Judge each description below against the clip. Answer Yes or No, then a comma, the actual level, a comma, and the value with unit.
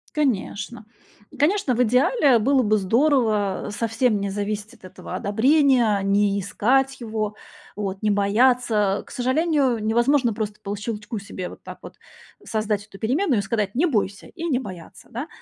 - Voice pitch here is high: Yes, high, 220 Hz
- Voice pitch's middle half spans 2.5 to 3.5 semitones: No, average, 4.1 semitones